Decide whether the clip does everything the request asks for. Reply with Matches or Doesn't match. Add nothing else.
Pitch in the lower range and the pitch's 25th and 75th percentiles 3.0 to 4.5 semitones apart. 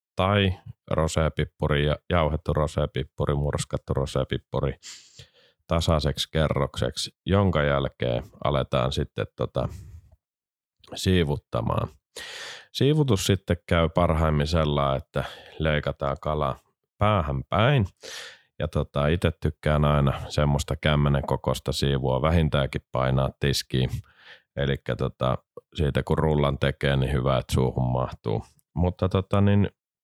Matches